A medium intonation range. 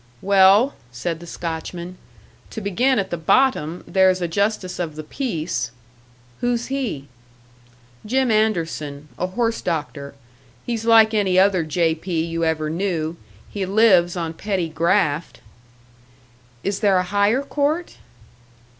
Yes: average, 4.8 semitones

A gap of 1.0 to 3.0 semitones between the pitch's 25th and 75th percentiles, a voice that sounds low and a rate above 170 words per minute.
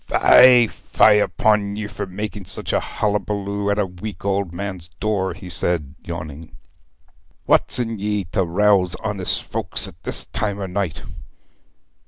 No: narrow, 2.5 semitones; low, 100 Hz; average, 155 wpm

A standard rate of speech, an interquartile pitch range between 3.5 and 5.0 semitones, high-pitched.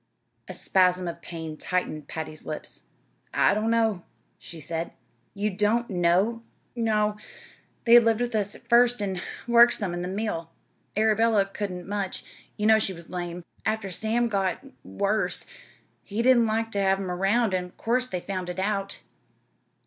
Yes: average, 160 wpm; average, 3.8 semitones; high, 200 Hz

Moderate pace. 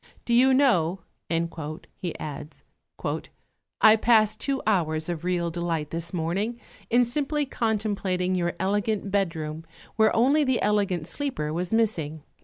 No: slow, 130 wpm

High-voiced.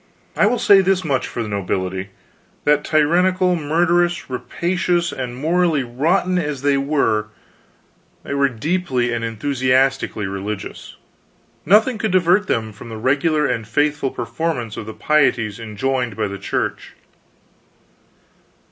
No: medium, 140 Hz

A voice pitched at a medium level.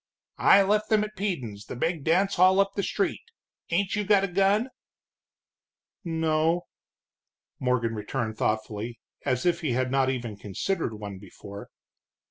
Yes: medium, 160 Hz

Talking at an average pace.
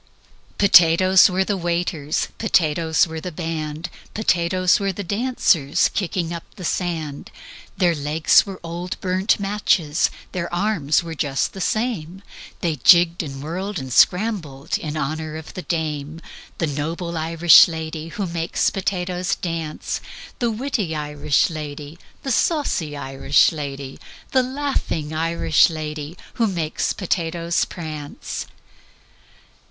No: slow, 125 wpm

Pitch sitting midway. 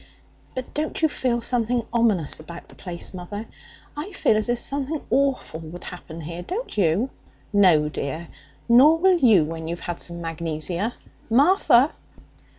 No: high, 210 Hz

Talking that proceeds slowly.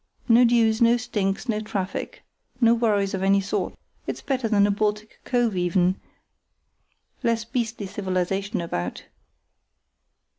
Yes: slow, 125 wpm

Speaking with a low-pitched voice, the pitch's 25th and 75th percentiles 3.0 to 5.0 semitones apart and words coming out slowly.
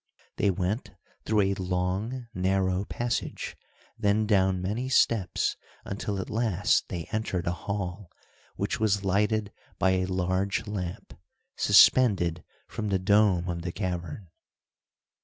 No: very low, 95 Hz; narrow, 2.5 semitones; slow, 125 wpm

